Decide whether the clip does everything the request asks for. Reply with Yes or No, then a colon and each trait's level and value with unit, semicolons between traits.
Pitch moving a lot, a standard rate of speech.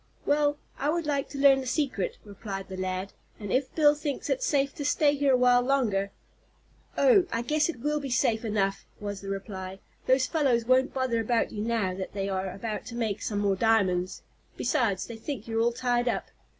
No: wide, 5.7 semitones; fast, 210 wpm